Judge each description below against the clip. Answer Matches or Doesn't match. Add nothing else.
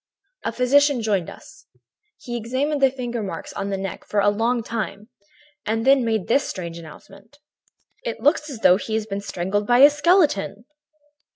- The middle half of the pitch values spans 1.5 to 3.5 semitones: Doesn't match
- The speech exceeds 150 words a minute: Matches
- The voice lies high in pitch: Matches